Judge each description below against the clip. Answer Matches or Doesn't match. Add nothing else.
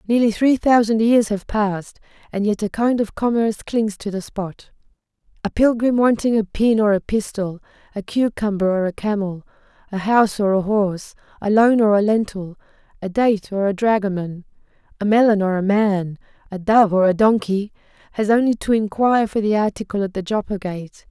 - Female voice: Matches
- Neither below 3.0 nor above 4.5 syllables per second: Doesn't match